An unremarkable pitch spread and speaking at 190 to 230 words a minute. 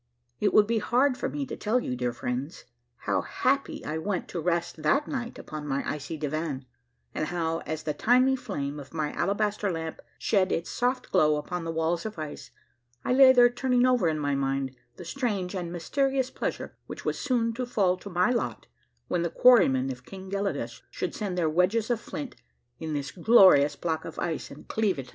No: wide, 7.3 semitones; fast, 205 wpm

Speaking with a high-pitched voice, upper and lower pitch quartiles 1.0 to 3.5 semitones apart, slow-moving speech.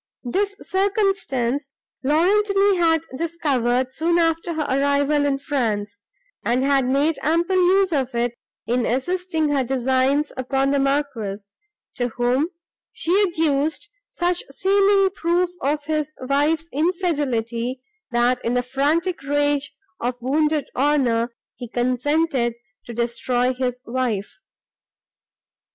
No: very high, 280 Hz; average, 4.8 semitones; slow, 115 wpm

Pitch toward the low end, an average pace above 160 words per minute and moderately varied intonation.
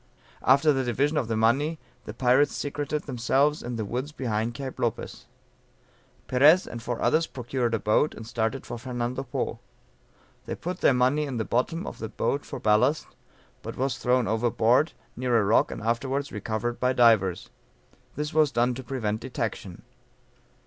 Yes: low, 125 Hz; average, 170 wpm; average, 3.5 semitones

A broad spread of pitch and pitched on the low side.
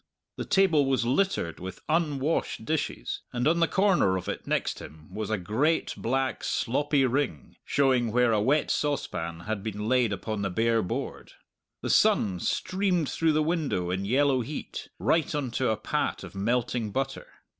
Yes: wide, 6.1 semitones; low, 125 Hz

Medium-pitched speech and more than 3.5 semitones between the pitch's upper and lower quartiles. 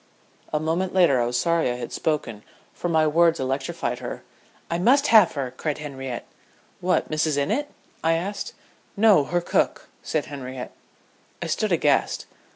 Yes: medium, 155 Hz; average, 4.5 semitones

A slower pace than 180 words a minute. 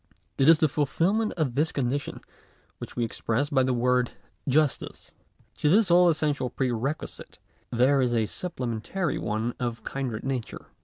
Yes: average, 155 wpm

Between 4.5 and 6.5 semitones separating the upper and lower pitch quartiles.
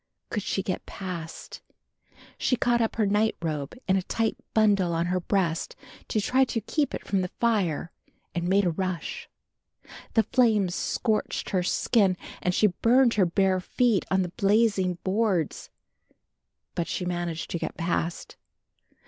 No: average, 3.8 semitones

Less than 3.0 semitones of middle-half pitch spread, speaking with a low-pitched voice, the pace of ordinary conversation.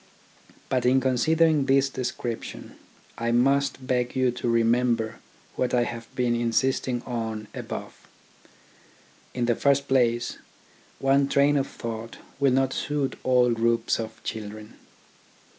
No: narrow, 2.4 semitones; low, 125 Hz; slow, 125 wpm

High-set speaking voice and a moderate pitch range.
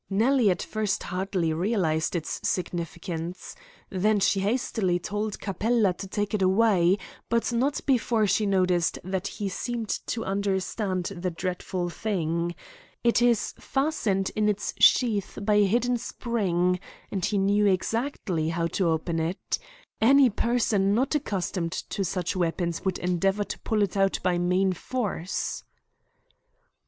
Yes: high, 195 Hz; average, 3.4 semitones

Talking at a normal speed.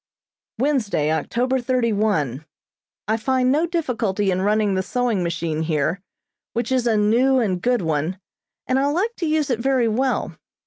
Yes: average, 165 wpm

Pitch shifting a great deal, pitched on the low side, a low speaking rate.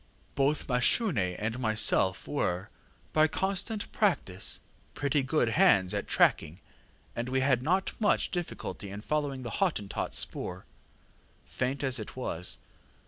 Yes: wide, 6.7 semitones; low, 130 Hz; slow, 130 wpm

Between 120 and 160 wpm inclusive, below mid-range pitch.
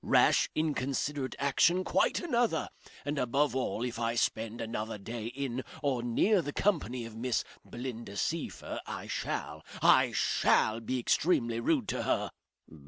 Yes: average, 145 wpm; low, 125 Hz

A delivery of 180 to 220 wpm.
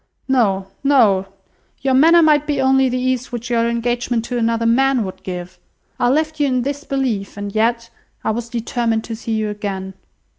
Yes: average, 185 wpm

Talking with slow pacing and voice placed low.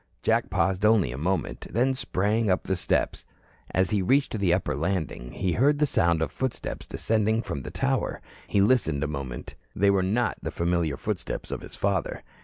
No: average, 190 wpm; very low, 95 Hz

